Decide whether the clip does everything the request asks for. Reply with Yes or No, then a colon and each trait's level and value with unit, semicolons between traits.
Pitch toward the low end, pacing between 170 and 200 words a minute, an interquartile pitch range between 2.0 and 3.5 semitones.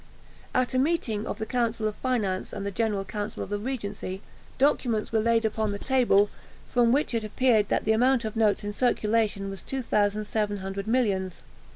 No: high, 220 Hz; average, 180 wpm; average, 2.9 semitones